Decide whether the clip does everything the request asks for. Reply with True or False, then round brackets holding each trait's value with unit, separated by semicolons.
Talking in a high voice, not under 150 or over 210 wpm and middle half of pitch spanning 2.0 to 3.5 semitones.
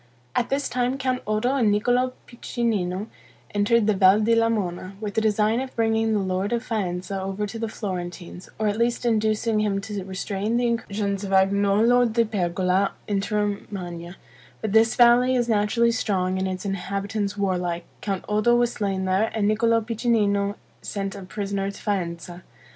True (210 Hz; 170 wpm; 2.8 semitones)